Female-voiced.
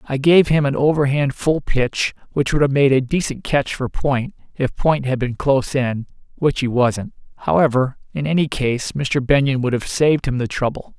No: male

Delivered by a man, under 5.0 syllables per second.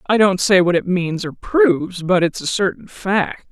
No: female; 4.5 syllables/s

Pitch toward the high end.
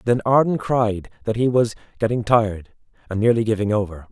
No: low, 110 Hz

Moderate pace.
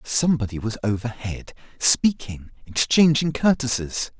No: slow, 70 wpm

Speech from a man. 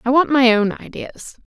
No: female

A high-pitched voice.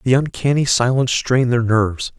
No: low, 125 Hz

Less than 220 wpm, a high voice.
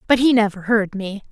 No: fast, 230 wpm; high, 215 Hz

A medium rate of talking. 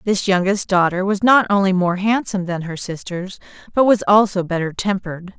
Yes: average, 180 wpm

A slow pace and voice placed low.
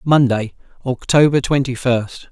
Yes: slow, 105 wpm; low, 130 Hz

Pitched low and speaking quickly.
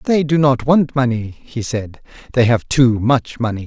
No: low, 125 Hz; average, 195 wpm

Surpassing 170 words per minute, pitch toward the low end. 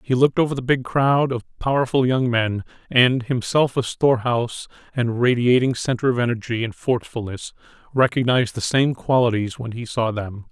No: average, 165 wpm; low, 120 Hz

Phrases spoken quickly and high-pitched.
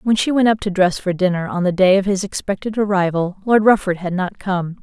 Yes: fast, 250 wpm; high, 195 Hz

